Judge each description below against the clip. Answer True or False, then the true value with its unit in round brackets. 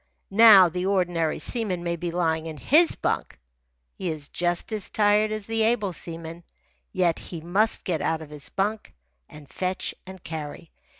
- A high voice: False (180 Hz)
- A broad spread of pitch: False (4.1 semitones)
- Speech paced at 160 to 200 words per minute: True (170 wpm)